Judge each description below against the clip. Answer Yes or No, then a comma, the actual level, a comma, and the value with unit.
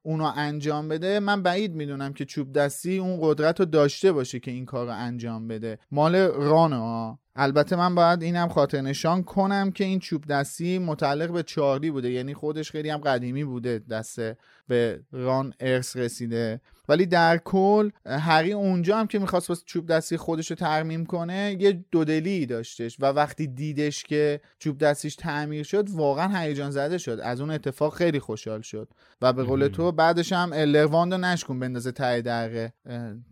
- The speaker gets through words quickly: Yes, fast, 175 wpm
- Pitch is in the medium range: Yes, medium, 150 Hz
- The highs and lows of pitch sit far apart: No, average, 4.9 semitones